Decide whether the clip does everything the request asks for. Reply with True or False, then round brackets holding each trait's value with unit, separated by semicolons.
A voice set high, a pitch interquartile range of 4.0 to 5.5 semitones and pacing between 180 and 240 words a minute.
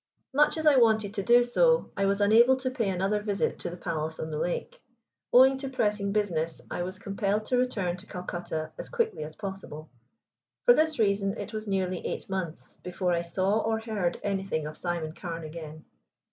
True (195 Hz; 4.3 semitones; 195 wpm)